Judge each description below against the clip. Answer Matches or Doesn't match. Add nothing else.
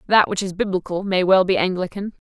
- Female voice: Matches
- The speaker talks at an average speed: Doesn't match